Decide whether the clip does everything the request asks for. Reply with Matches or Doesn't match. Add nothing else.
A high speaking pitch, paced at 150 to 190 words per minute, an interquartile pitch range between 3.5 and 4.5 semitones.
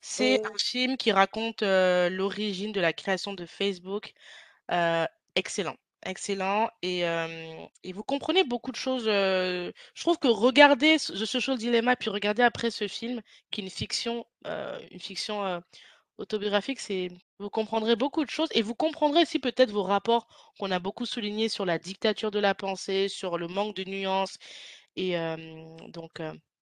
Matches